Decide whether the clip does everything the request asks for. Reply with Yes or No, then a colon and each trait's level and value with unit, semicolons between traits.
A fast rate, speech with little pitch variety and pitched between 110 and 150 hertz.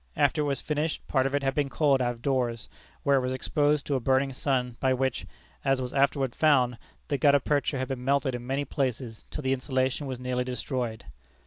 Yes: fast, 220 wpm; narrow, 1.9 semitones; low, 135 Hz